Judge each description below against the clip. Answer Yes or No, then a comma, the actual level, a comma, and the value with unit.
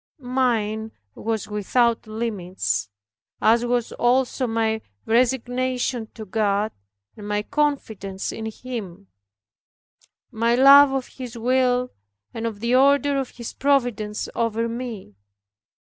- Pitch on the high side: Yes, high, 230 Hz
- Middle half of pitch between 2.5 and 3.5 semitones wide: Yes, average, 2.9 semitones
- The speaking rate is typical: No, slow, 115 wpm